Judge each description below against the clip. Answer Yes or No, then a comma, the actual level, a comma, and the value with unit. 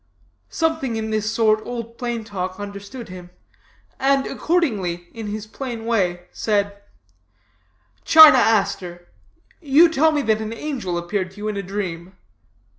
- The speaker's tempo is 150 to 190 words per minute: No, average, 140 wpm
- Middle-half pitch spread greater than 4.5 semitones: No, average, 4.1 semitones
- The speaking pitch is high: Yes, high, 215 Hz